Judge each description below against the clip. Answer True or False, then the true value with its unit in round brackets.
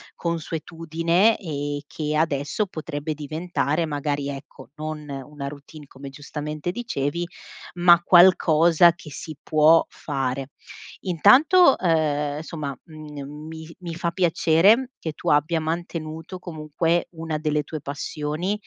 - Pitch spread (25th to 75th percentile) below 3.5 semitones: True (2.6 semitones)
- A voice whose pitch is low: False (155 Hz)